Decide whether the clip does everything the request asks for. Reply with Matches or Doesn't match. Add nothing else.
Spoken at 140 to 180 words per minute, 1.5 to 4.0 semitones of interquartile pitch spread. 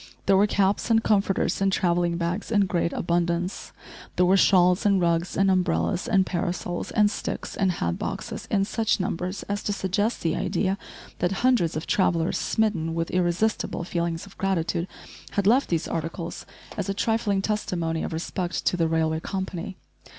Matches